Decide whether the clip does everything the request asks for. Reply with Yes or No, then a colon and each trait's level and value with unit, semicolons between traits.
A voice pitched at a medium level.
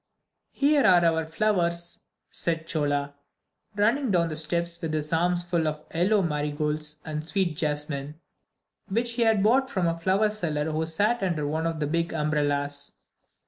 Yes: medium, 165 Hz